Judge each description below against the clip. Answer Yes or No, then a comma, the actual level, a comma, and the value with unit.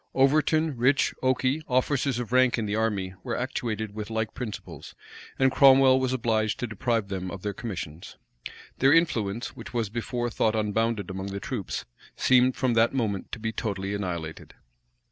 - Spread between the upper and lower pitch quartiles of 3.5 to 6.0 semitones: Yes, average, 4.0 semitones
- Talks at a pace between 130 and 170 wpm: Yes, average, 165 wpm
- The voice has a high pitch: No, low, 115 Hz